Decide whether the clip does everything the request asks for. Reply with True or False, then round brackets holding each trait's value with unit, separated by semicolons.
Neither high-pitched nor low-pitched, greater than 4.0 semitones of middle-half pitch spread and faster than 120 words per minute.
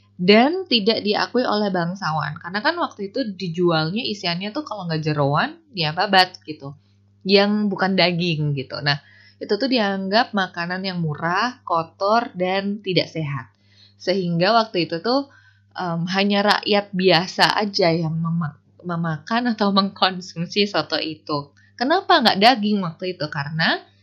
True (180 Hz; 4.7 semitones; 135 wpm)